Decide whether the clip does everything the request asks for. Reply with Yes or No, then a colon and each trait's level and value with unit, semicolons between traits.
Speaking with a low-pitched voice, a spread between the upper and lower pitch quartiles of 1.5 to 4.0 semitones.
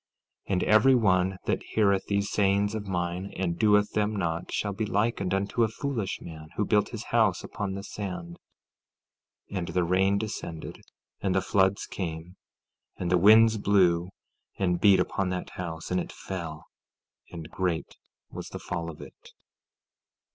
Yes: very low, 95 Hz; average, 2.7 semitones